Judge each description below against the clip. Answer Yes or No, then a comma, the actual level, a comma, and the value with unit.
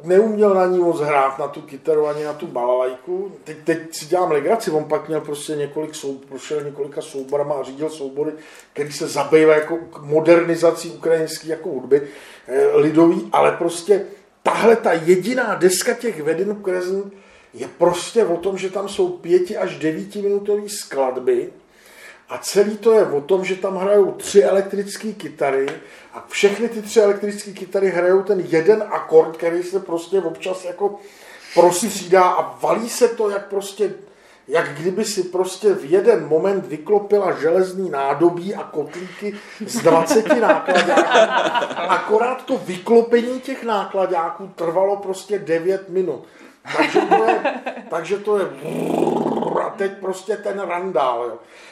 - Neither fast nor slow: Yes, average, 150 wpm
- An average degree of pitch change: Yes, average, 4.3 semitones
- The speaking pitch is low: No, high, 190 Hz